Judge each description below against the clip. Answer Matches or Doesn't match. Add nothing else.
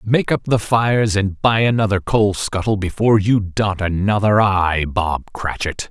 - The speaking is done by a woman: Doesn't match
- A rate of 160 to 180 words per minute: Matches